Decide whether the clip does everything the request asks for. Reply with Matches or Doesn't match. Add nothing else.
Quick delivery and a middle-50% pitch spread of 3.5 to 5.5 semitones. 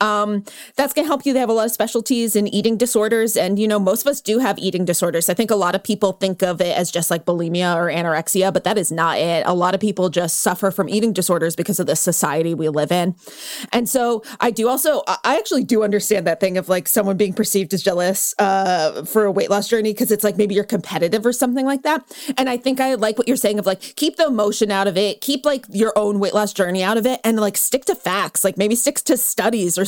Matches